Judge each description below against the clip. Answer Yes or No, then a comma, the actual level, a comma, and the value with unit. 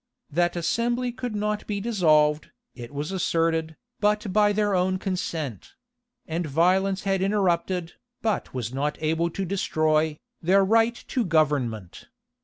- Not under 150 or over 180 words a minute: No, slow, 135 wpm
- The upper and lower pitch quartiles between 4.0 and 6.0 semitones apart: Yes, average, 4.7 semitones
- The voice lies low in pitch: No, medium, 180 Hz